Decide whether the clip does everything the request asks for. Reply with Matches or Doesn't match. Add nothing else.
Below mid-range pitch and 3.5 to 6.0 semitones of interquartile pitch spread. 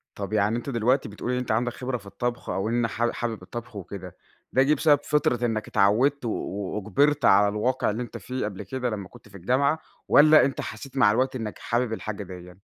Matches